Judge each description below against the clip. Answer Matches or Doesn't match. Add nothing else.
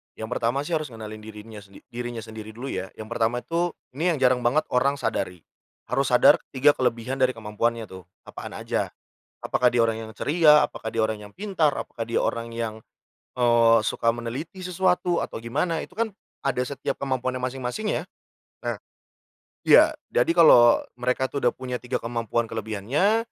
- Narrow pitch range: Doesn't match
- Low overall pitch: Matches